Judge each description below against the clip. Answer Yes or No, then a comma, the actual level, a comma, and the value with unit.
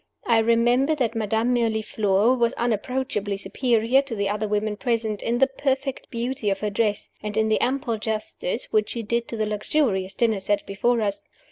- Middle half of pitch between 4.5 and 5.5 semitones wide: No, average, 2.7 semitones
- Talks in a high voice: Yes, high, 225 Hz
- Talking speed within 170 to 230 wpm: Yes, average, 180 wpm